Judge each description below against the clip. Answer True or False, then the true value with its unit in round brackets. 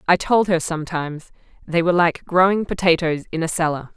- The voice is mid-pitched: True (170 Hz)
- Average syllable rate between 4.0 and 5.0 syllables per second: False (5.8 syllables/s)